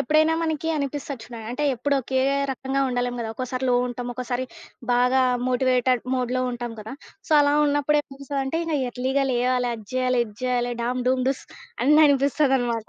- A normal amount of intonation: No, narrow, 2.2 semitones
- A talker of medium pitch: No, very high, 255 Hz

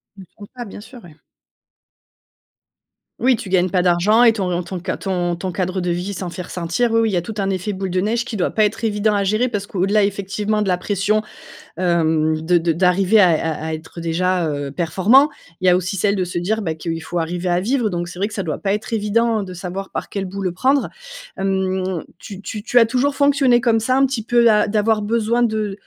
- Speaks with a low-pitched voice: No, high, 195 Hz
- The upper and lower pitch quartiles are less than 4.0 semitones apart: Yes, average, 3.6 semitones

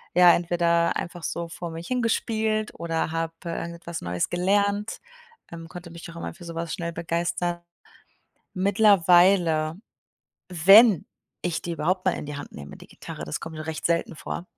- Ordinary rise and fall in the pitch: No, narrow, 1.9 semitones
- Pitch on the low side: No, medium, 170 Hz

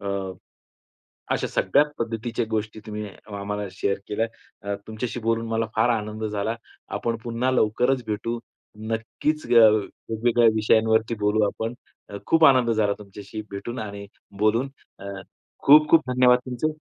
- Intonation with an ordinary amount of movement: No, narrow, 2.3 semitones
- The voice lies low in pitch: Yes, low, 110 Hz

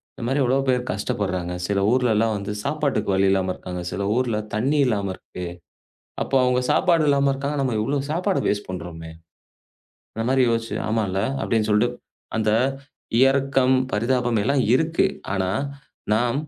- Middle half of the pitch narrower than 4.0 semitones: No, average, 5.0 semitones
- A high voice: No, low, 120 Hz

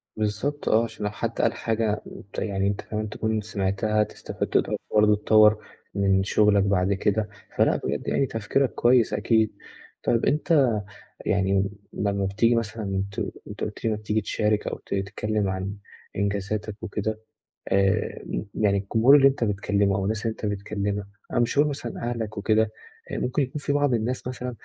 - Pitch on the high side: No, low, 105 Hz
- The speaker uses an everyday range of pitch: No, narrow, 2.3 semitones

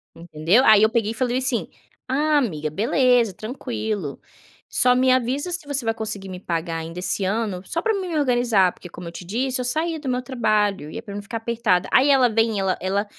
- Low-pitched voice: No, high, 225 Hz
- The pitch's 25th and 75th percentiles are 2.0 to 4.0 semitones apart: No, average, 5.1 semitones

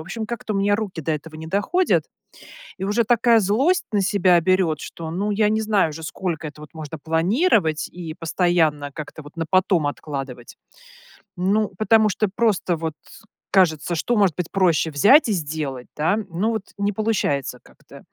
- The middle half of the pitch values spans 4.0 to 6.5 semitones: Yes, average, 5.0 semitones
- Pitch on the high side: No, medium, 180 Hz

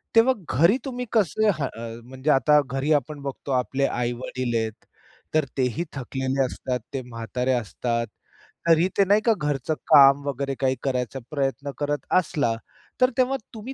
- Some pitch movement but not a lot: Yes, average, 3.7 semitones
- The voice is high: No, low, 135 Hz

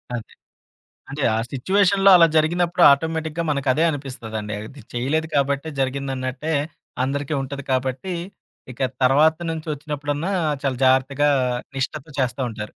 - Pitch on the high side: No, medium, 140 Hz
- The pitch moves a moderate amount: Yes, average, 3.3 semitones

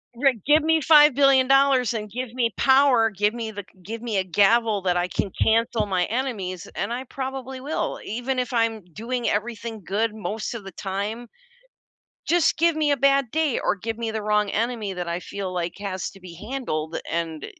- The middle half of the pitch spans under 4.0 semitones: No, average, 4.5 semitones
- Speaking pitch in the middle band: No, high, 225 Hz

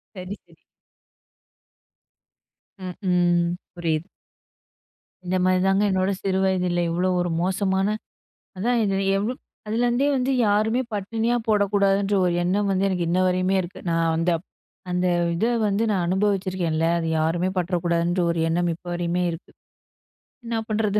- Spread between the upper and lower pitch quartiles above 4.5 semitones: No, average, 2.7 semitones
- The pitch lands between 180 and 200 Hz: Yes, medium, 185 Hz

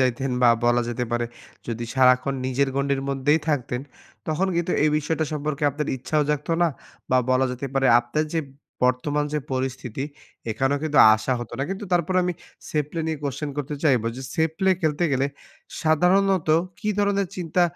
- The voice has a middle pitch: Yes, medium, 145 Hz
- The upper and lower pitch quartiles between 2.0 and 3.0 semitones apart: No, average, 3.7 semitones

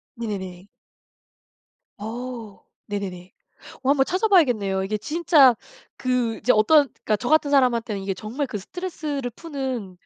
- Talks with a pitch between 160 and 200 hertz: No, high, 240 Hz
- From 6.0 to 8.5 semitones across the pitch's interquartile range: No, wide, 5.5 semitones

